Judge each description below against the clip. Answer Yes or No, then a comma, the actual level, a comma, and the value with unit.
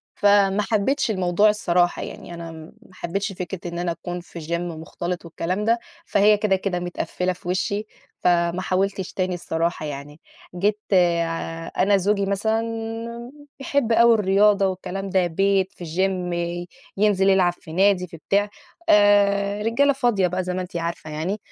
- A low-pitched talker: No, high, 190 Hz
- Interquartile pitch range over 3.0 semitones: No, narrow, 2.6 semitones